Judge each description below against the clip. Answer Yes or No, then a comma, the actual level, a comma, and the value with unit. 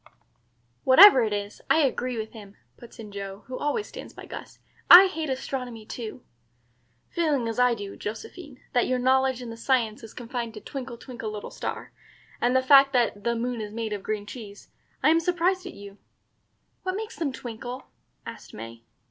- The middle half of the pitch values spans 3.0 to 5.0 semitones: Yes, average, 3.9 semitones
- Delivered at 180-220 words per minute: Yes, average, 185 wpm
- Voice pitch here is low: No, high, 245 Hz